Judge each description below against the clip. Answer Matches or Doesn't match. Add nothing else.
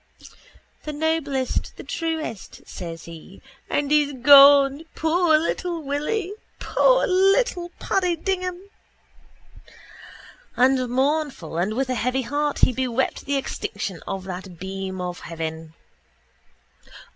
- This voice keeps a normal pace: Doesn't match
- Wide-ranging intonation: Matches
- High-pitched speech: Matches